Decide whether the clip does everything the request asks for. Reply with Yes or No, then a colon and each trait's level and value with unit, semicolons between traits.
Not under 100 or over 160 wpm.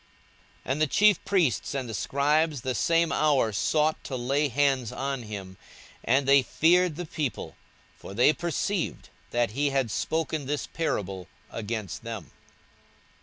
Yes: average, 150 wpm